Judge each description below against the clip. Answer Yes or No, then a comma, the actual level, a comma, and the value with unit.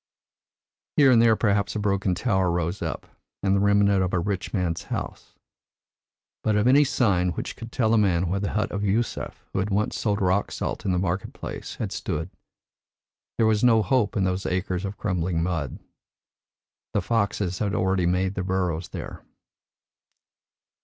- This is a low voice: Yes, very low, 95 Hz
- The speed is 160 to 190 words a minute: Yes, average, 175 wpm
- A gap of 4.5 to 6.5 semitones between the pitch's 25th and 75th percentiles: No, narrow, 2.5 semitones